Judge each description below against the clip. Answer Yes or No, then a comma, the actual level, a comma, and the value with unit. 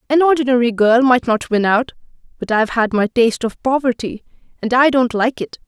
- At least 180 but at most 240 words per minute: Yes, average, 200 wpm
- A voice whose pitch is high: Yes, high, 240 Hz